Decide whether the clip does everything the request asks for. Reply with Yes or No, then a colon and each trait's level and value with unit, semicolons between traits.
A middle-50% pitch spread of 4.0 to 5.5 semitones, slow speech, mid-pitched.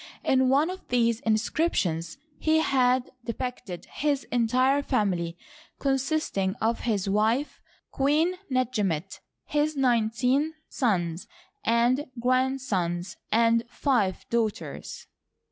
No: average, 4.4 semitones; slow, 100 wpm; high, 245 Hz